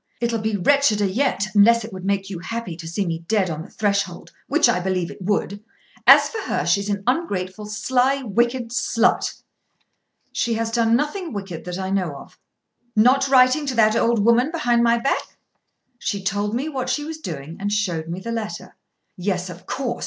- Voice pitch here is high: Yes, high, 215 Hz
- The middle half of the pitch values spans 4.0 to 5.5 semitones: Yes, average, 4.3 semitones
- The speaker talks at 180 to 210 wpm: Yes, average, 190 wpm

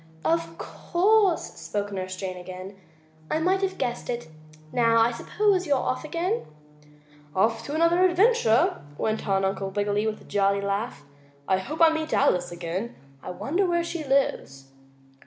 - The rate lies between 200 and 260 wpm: No, average, 160 wpm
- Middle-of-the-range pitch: No, high, 230 Hz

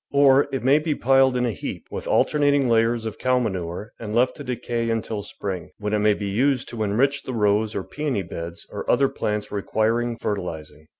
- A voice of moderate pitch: No, low, 115 Hz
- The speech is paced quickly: Yes, fast, 215 wpm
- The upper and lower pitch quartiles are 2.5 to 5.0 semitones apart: Yes, average, 4.2 semitones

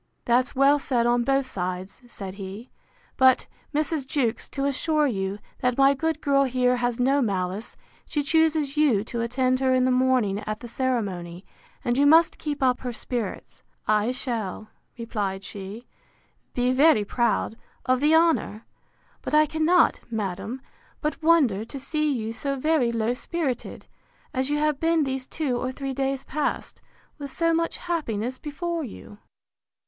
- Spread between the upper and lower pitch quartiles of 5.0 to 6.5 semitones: No, average, 4.3 semitones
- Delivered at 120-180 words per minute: Yes, average, 160 wpm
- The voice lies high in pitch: Yes, very high, 255 Hz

